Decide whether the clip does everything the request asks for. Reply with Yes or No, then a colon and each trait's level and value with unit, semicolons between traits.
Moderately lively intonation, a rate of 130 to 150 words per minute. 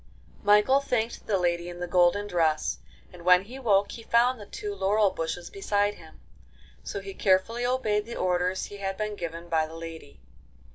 No: average, 3.4 semitones; average, 185 wpm